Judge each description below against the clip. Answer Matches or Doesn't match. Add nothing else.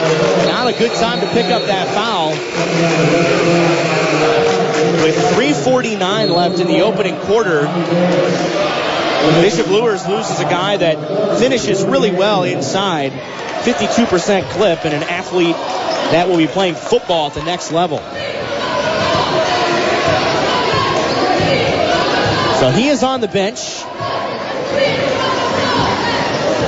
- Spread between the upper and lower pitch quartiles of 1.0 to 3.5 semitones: Doesn't match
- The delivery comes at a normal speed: Doesn't match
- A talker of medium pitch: Matches